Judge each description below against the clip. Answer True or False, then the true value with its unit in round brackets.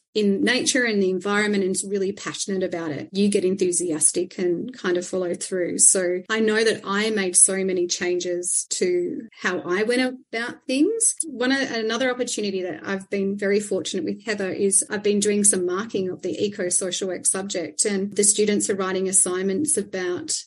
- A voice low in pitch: False (195 Hz)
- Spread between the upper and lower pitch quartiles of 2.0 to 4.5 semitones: True (3.1 semitones)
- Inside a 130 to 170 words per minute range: False (185 wpm)